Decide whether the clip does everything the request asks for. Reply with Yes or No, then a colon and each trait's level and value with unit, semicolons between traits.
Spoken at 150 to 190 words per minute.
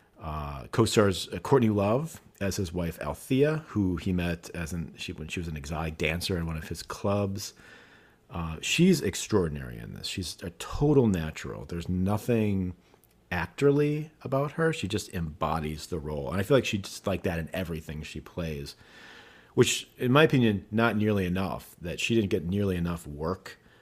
Yes: average, 175 wpm